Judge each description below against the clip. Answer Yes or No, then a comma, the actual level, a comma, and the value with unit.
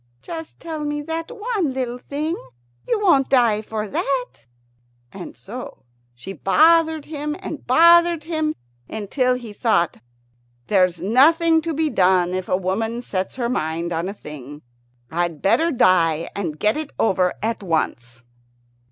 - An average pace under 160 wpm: Yes, average, 145 wpm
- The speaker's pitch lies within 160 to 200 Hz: No, high, 240 Hz